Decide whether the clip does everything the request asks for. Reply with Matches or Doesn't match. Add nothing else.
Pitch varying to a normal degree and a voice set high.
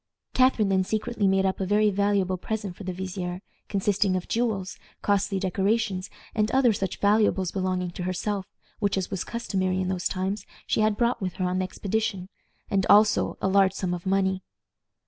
Doesn't match